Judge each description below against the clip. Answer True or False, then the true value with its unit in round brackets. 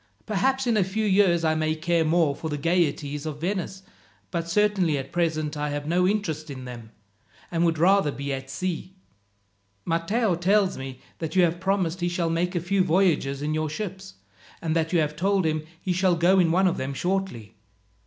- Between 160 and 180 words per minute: False (200 wpm)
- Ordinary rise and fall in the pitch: True (3.5 semitones)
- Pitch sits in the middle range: True (170 Hz)